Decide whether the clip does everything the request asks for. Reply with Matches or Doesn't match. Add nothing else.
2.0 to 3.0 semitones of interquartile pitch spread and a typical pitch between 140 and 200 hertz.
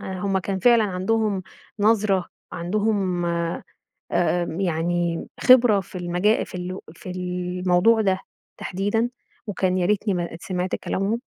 Matches